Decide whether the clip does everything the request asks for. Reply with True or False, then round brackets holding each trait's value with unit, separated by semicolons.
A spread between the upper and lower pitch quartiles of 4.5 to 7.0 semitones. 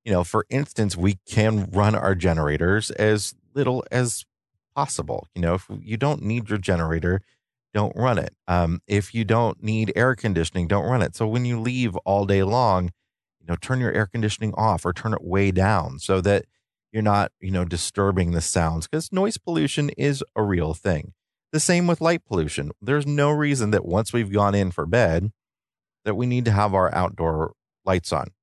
True (4.8 semitones)